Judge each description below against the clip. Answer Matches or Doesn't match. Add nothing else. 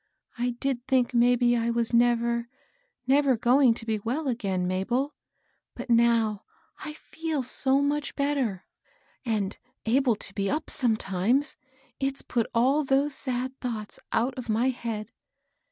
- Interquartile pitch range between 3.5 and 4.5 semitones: Doesn't match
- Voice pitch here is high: Matches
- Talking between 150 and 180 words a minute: Doesn't match